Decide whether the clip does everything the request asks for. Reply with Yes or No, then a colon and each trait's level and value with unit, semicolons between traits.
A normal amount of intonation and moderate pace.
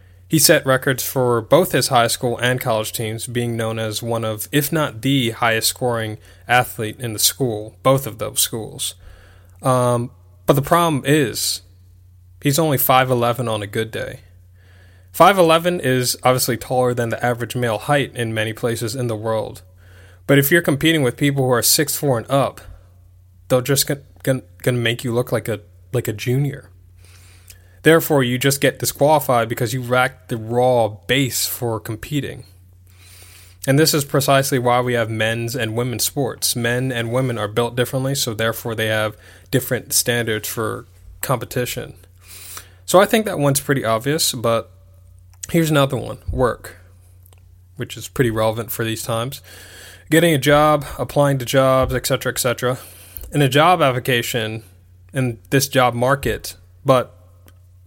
No: wide, 5.9 semitones; average, 160 wpm